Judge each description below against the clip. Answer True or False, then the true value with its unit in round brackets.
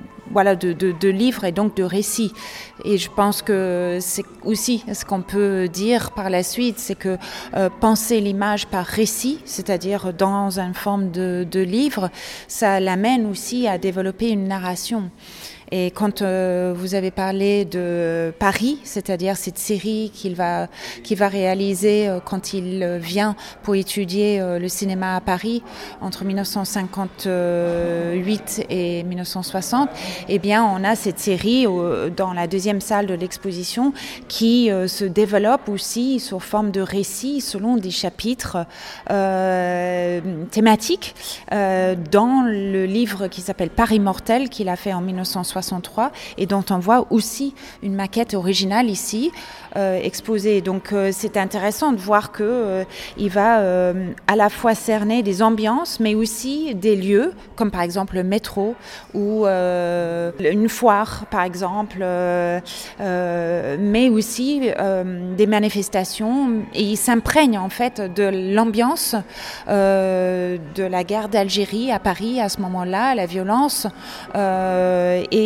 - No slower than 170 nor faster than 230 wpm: False (145 wpm)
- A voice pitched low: False (200 Hz)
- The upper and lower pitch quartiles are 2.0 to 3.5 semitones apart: True (2.7 semitones)